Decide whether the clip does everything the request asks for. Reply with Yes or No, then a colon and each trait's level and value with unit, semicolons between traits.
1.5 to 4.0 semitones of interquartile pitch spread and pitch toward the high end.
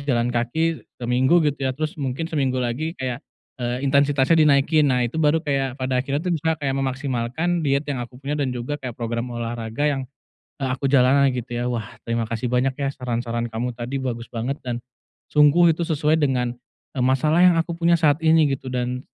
No: average, 3.3 semitones; low, 135 Hz